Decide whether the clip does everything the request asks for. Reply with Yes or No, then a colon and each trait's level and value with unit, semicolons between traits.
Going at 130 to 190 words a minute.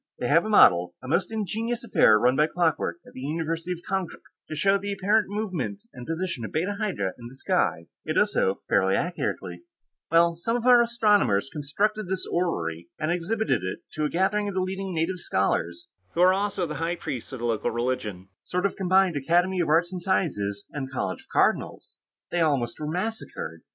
No: average, 200 wpm